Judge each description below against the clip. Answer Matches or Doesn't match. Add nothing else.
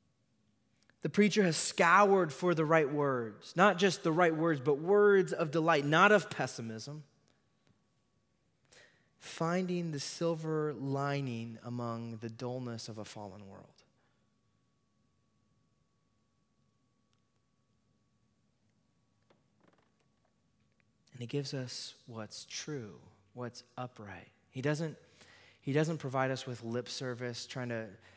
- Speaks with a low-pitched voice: Matches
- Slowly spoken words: Matches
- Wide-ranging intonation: Matches